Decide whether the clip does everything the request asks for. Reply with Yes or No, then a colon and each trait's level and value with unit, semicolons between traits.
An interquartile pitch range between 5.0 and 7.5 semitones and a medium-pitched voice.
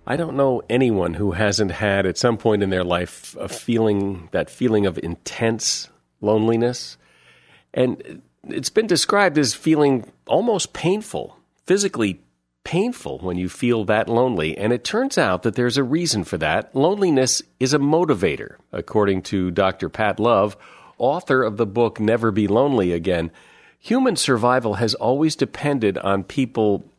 No: wide, 5.6 semitones; low, 115 Hz